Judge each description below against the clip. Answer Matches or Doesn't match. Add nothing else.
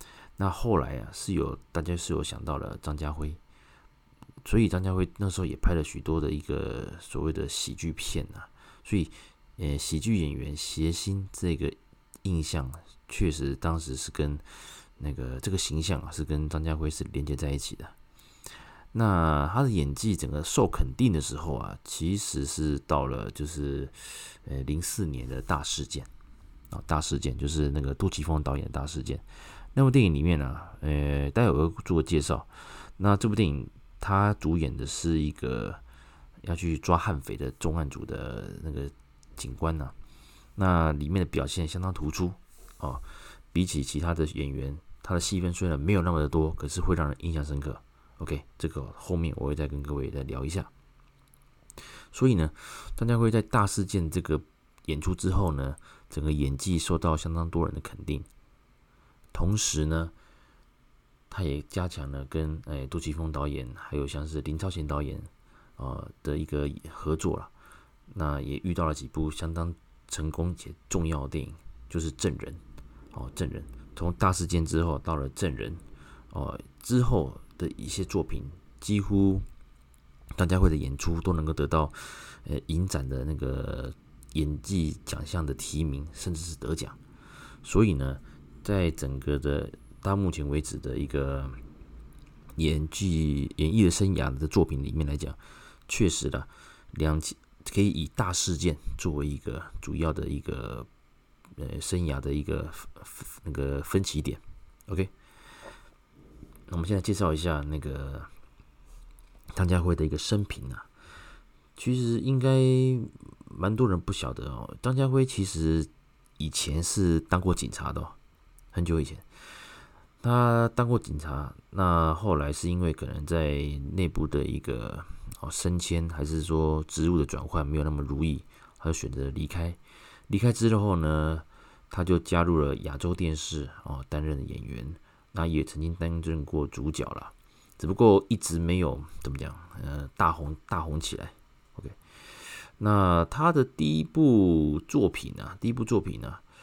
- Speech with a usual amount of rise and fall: Matches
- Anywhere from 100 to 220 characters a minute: Doesn't match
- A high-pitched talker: Doesn't match